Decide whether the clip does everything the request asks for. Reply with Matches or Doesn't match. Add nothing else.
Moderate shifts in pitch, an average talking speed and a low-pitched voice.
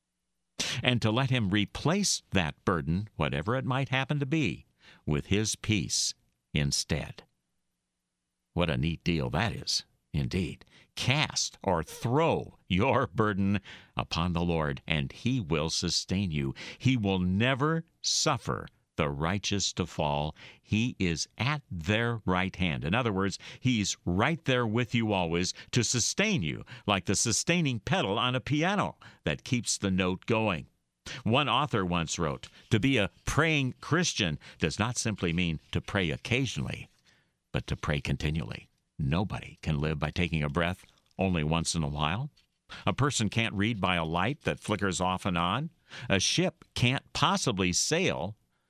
Doesn't match